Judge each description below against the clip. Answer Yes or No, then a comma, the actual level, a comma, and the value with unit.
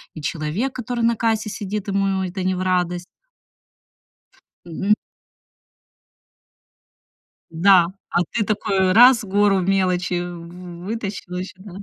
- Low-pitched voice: No, high, 190 Hz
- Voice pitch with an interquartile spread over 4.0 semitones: No, average, 2.8 semitones